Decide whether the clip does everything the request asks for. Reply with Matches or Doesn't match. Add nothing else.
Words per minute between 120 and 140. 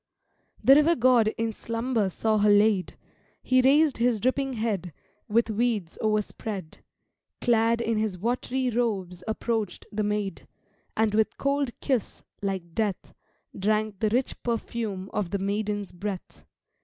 Matches